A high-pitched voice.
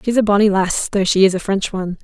Yes: high, 195 Hz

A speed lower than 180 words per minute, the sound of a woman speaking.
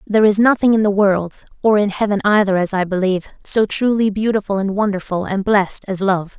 No: average, 190 wpm; female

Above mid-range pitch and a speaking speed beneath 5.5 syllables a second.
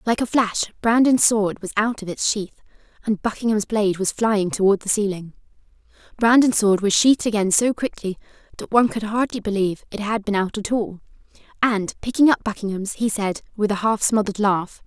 No: high, 210 Hz; 5.6 syllables/s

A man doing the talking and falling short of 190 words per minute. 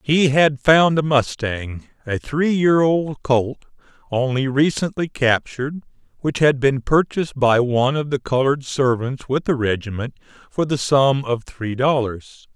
Yes: male; average, 155 wpm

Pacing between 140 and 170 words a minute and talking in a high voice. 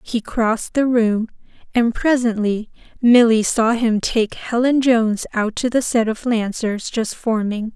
Yes: average, 155 wpm; high, 230 Hz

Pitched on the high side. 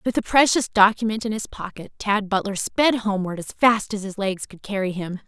Yes: high, 205 Hz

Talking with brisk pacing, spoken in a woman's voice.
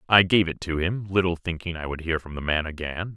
No: fast, 265 wpm; male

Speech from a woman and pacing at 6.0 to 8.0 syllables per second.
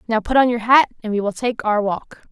No: female; 5.6 syllables/s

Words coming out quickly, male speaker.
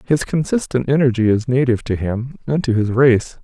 No: average, 190 wpm; male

